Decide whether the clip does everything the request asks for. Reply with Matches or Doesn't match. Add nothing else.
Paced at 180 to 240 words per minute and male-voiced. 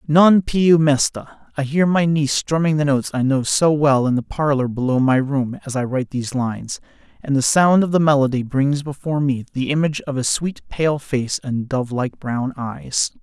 Matches